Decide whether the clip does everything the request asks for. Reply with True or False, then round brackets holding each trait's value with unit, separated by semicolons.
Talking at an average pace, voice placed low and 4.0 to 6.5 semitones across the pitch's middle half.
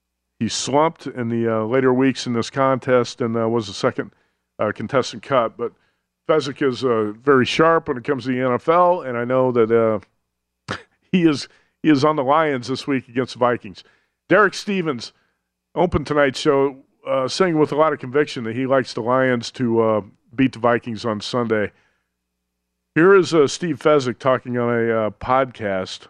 True (185 wpm; 125 Hz; 4.3 semitones)